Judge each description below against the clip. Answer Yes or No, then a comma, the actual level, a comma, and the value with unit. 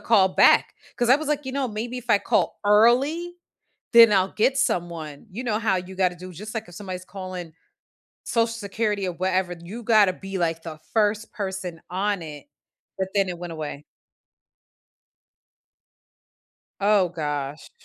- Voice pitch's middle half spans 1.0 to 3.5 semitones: No, average, 4.1 semitones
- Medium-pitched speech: No, high, 195 Hz